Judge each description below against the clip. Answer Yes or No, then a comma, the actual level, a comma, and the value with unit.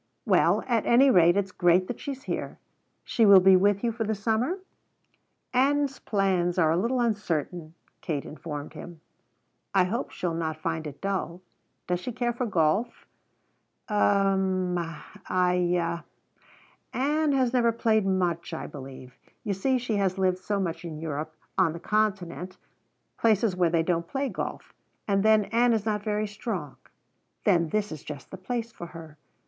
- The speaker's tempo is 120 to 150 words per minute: No, average, 165 wpm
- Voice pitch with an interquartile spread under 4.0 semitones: No, average, 4.7 semitones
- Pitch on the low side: No, high, 190 Hz